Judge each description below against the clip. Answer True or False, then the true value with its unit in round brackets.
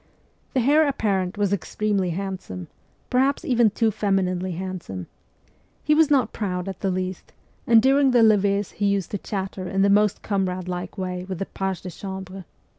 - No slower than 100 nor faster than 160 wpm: False (180 wpm)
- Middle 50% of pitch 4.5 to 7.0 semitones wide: False (2.6 semitones)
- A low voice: False (195 Hz)